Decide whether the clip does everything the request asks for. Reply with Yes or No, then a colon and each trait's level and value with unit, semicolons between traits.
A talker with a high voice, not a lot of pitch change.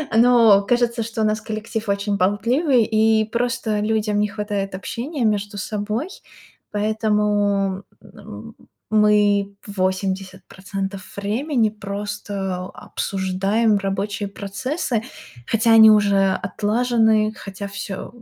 Yes: high, 210 Hz; narrow, 2.0 semitones